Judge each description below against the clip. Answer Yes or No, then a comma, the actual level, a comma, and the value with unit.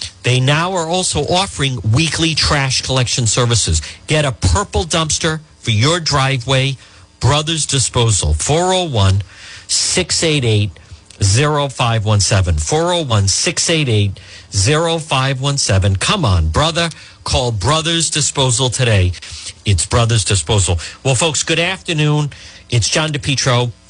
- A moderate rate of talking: No, slow, 105 wpm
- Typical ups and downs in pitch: No, wide, 7.1 semitones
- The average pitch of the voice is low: Yes, low, 125 Hz